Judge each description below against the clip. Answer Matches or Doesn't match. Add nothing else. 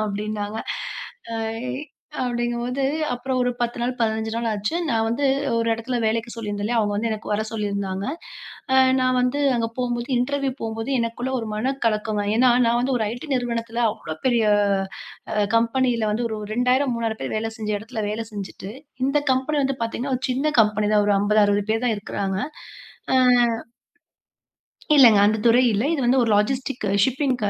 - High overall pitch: Matches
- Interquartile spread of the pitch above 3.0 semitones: Doesn't match